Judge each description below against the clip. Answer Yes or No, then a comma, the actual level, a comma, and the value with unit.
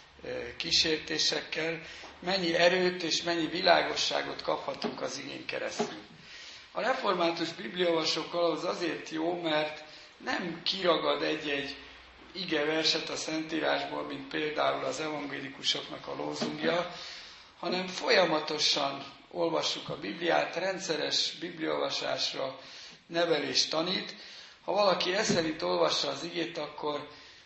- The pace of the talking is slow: Yes, slow, 100 wpm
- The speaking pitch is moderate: Yes, medium, 160 Hz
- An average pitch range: No, narrow, 2.0 semitones